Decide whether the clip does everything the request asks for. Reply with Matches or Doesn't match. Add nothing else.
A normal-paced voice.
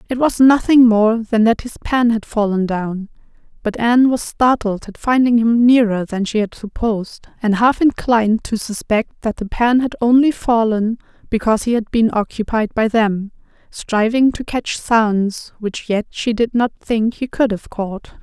Matches